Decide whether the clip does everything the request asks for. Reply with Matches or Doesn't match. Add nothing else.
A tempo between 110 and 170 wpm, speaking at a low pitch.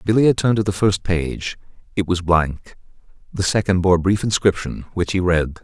Doesn't match